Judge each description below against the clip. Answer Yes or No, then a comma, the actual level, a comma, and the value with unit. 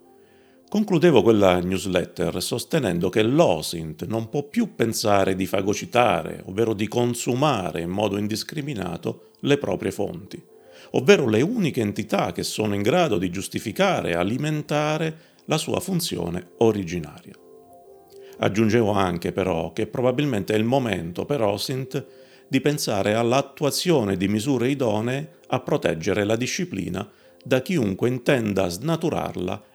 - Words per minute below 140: Yes, average, 125 wpm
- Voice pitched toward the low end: Yes, low, 115 Hz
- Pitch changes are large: Yes, wide, 6.8 semitones